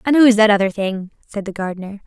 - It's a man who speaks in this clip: No, female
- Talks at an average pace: No, fast, 230 wpm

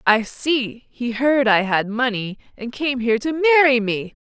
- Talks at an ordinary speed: Yes, average, 185 wpm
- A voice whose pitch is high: Yes, high, 245 Hz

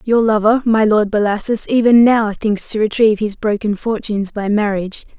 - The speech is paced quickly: No, average, 175 wpm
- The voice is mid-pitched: No, high, 215 Hz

